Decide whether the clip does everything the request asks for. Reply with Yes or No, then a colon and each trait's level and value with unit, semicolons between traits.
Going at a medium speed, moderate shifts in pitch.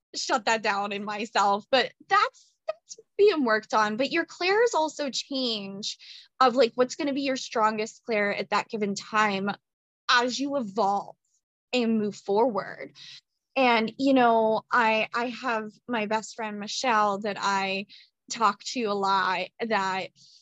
Yes: average, 155 wpm; average, 4.3 semitones